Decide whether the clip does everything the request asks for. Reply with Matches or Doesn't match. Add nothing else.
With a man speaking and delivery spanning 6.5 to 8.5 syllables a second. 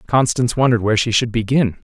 Matches